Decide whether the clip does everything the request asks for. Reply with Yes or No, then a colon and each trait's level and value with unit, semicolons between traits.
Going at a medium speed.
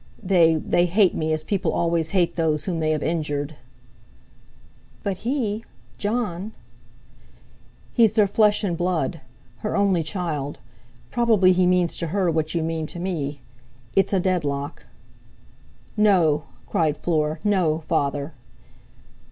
No: slow, 125 wpm